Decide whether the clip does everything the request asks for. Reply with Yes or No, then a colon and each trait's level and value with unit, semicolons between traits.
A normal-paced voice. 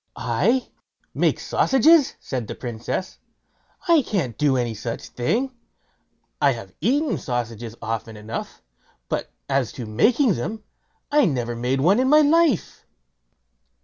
No: slow, 130 wpm